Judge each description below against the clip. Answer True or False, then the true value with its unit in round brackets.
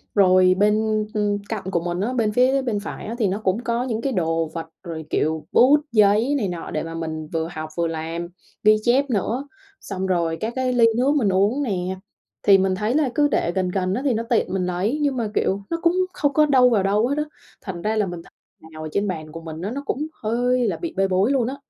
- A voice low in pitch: False (205 Hz)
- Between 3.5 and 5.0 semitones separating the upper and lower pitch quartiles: False (5.6 semitones)